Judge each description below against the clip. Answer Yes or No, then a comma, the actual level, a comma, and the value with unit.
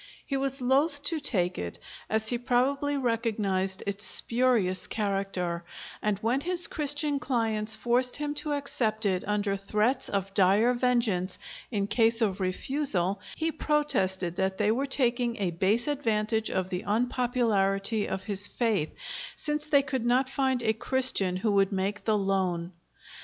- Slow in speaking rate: No, average, 150 wpm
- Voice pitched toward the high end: Yes, high, 220 Hz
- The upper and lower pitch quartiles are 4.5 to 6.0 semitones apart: Yes, average, 5.0 semitones